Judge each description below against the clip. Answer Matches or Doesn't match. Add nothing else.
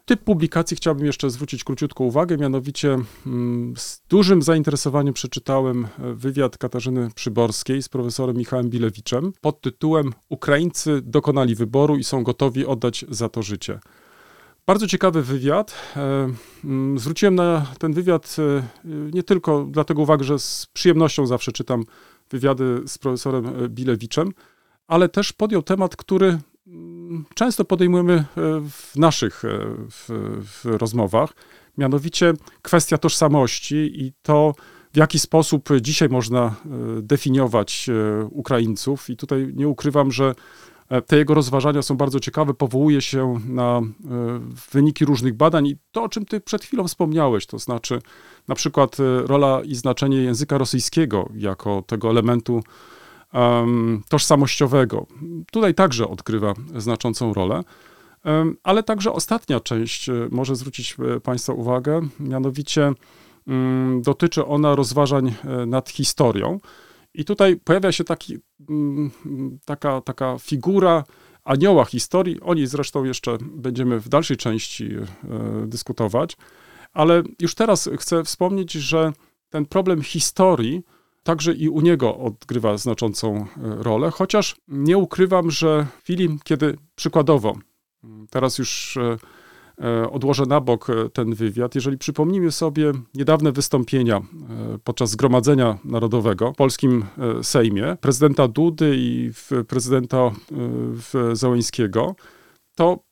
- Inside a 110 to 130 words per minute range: Matches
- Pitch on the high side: Doesn't match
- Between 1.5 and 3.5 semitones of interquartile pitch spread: Doesn't match